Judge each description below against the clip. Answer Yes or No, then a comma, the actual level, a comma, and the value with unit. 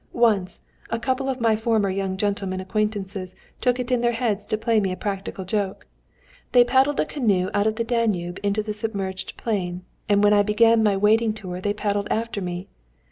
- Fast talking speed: No, average, 195 wpm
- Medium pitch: No, high, 210 Hz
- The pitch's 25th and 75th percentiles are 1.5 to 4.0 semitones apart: Yes, average, 2.9 semitones